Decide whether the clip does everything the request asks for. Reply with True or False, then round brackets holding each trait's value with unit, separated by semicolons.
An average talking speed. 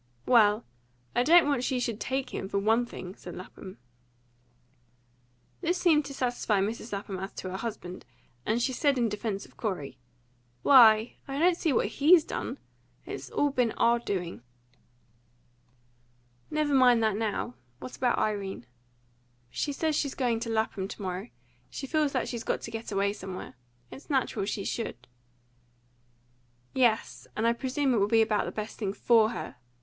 True (165 wpm)